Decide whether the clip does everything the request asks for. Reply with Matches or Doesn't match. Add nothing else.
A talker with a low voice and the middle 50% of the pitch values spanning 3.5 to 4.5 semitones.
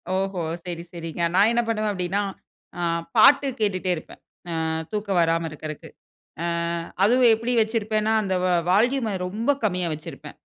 Doesn't match